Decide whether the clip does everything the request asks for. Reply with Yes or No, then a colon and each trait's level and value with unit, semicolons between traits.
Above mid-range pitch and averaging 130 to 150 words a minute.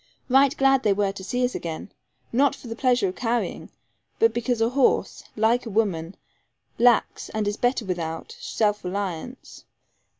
No: high, 225 Hz; average, 165 wpm